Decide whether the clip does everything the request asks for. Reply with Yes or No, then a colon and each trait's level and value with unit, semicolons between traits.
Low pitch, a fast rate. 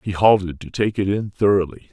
Yes: very low, 95 Hz; fast, 220 wpm